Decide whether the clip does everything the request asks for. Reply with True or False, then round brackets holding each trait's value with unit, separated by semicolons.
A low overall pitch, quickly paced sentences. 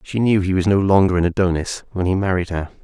True (95 Hz; 255 wpm)